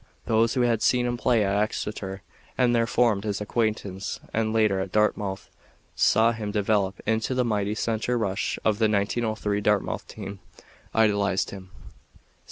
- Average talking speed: Yes, average, 155 wpm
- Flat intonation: Yes, narrow, 2.2 semitones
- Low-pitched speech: Yes, low, 105 Hz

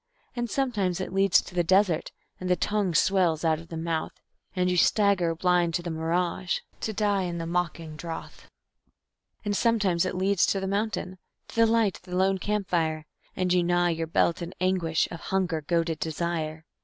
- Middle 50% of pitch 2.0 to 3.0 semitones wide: Yes, average, 2.7 semitones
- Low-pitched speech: No, medium, 180 Hz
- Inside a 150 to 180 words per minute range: No, average, 195 wpm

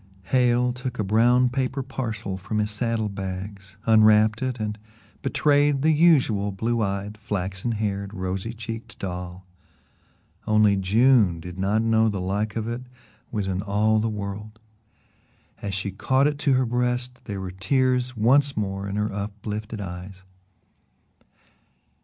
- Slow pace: No, average, 145 wpm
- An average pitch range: Yes, average, 3.8 semitones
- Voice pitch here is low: Yes, low, 110 Hz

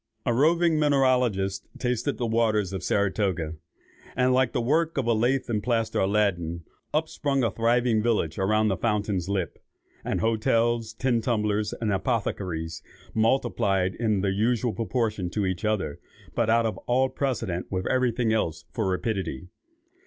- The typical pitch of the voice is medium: No, low, 110 Hz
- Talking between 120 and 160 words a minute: Yes, average, 155 wpm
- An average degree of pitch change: Yes, average, 4.0 semitones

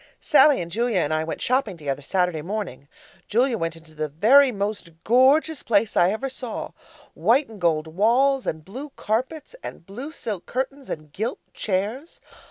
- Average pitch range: No, wide, 7.6 semitones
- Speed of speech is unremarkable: Yes, average, 170 wpm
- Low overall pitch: No, high, 215 Hz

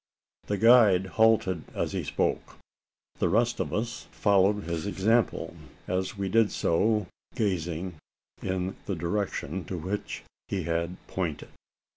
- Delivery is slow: Yes, slow, 130 wpm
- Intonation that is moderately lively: Yes, average, 3.0 semitones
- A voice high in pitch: No, very low, 95 Hz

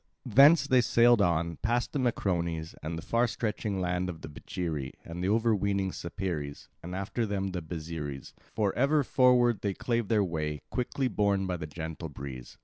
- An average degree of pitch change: No, wide, 6.0 semitones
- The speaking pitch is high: No, very low, 95 Hz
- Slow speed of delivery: No, average, 175 wpm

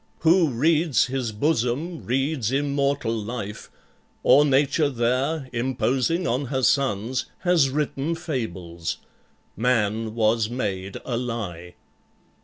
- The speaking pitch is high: No, low, 130 Hz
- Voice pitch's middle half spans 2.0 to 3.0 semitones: No, average, 4.2 semitones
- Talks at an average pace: No, slow, 105 wpm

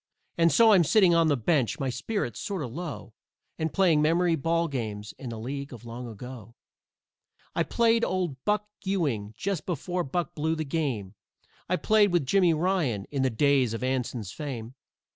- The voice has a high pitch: No, medium, 150 Hz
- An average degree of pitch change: No, wide, 6.2 semitones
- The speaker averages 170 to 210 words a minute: Yes, average, 180 wpm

